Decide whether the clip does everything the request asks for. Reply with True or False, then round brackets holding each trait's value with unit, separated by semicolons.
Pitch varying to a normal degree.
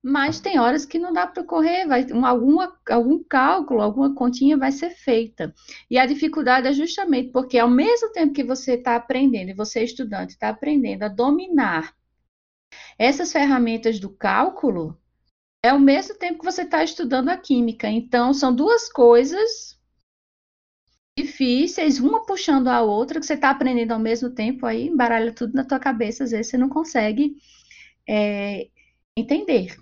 True (4.3 semitones)